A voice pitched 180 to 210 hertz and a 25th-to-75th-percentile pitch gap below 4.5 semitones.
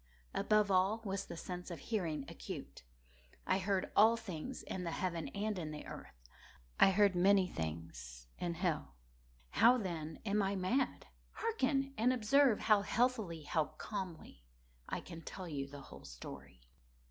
No: medium, 185 Hz; average, 5.1 semitones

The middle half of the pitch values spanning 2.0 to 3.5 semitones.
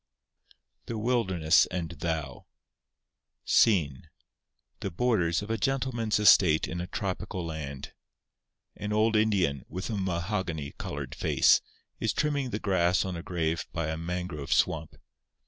No: average, 4.8 semitones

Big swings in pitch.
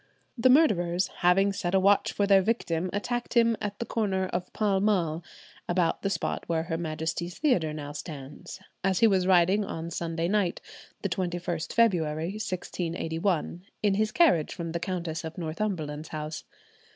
No: average, 3.6 semitones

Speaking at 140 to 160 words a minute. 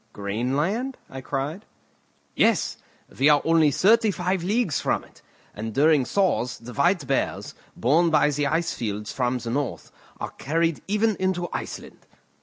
Yes: average, 150 wpm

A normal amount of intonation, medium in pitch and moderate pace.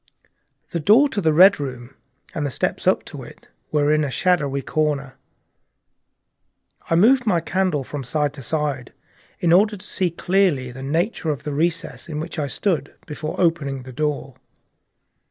Yes: average, 4.0 semitones; medium, 155 Hz; average, 170 wpm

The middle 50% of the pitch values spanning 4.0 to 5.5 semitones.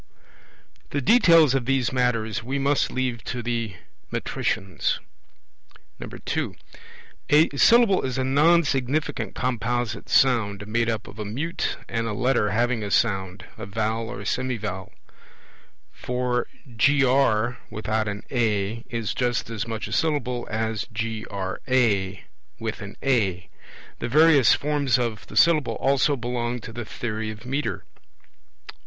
No: average, 3.6 semitones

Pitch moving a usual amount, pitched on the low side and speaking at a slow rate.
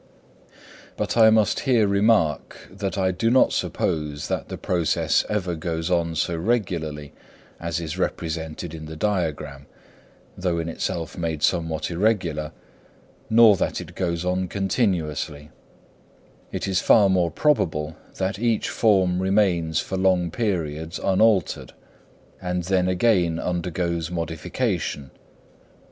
Yes: average, 3.2 semitones; very low, 90 Hz; slow, 125 wpm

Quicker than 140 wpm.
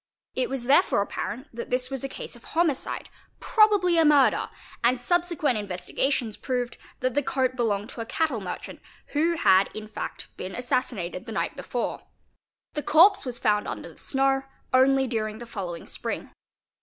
Yes: average, 170 wpm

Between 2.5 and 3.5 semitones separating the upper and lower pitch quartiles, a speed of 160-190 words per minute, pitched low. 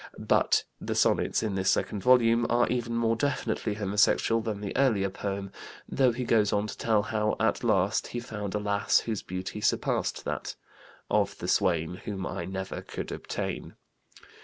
Yes: average, 2.9 semitones; average, 170 wpm; low, 105 Hz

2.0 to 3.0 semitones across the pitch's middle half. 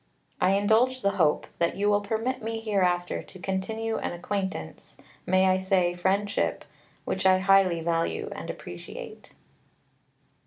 Yes: narrow, 2.4 semitones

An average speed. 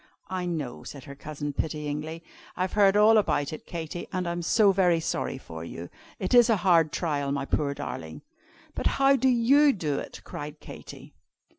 Yes: average, 180 wpm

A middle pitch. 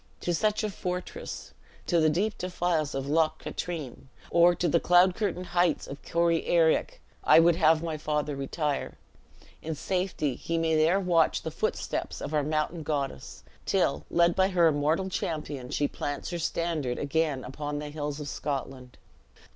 Yes: medium, 160 Hz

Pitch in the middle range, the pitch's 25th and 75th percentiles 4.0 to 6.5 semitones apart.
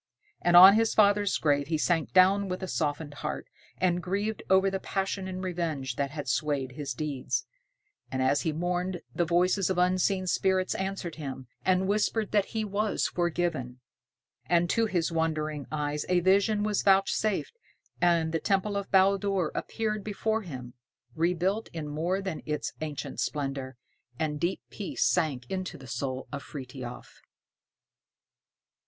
Yes: medium, 175 Hz; average, 4.5 semitones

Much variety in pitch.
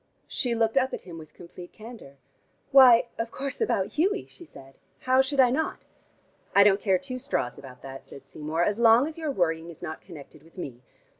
Yes: wide, 8.3 semitones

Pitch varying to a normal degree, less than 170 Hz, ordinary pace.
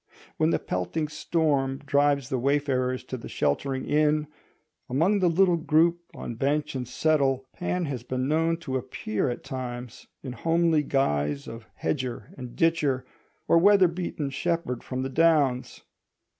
Yes: average, 4.2 semitones; medium, 140 Hz; average, 150 wpm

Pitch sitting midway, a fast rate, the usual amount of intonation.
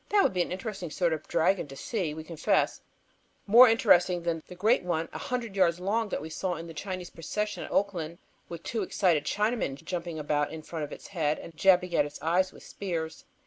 Yes: medium, 175 Hz; fast, 220 wpm; average, 3.5 semitones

